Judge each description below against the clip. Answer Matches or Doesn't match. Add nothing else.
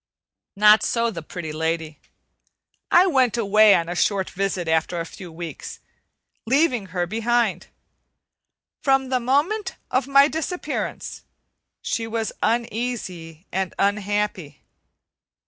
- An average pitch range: Doesn't match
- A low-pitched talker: Doesn't match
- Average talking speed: Doesn't match